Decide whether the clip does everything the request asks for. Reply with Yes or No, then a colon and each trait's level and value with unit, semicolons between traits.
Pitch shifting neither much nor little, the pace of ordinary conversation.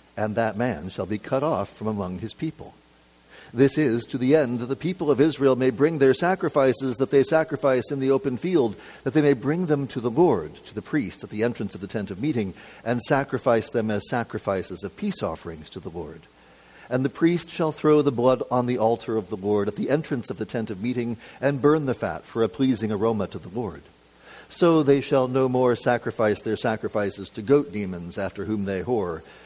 No: average, 4.8 semitones; fast, 220 wpm